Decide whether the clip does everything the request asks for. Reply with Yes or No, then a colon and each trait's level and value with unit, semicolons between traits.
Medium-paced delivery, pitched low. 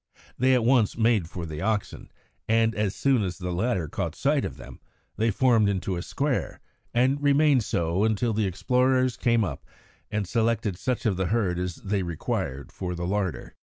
Yes: average, 185 wpm; low, 105 Hz